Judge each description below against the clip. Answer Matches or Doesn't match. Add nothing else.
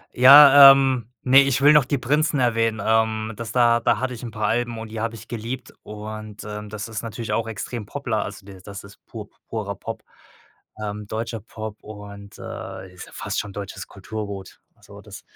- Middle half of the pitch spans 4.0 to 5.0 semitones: Doesn't match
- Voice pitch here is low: Matches